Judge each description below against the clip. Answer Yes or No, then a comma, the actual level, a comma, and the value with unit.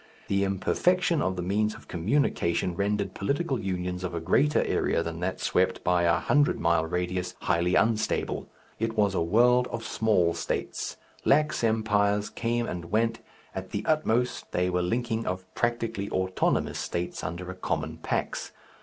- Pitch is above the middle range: No, low, 100 Hz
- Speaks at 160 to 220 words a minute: Yes, average, 165 wpm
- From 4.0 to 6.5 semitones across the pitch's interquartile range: Yes, average, 4.3 semitones